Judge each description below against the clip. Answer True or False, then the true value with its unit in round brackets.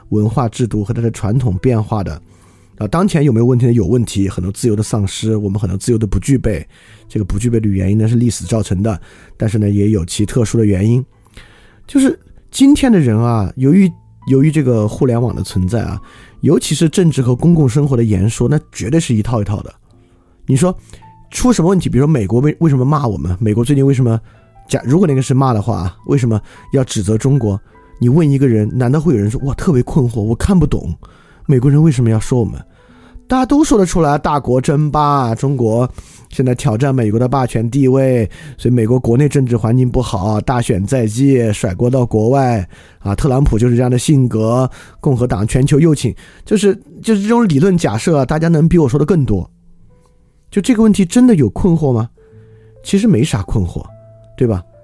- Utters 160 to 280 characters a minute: False (310 characters per minute)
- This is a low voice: True (120 Hz)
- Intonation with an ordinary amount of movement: True (4.6 semitones)